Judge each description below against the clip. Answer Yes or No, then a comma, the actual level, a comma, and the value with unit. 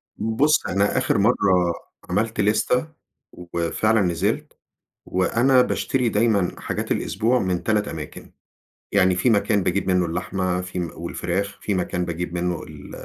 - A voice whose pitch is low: Yes, very low, 95 Hz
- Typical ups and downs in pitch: Yes, average, 3.7 semitones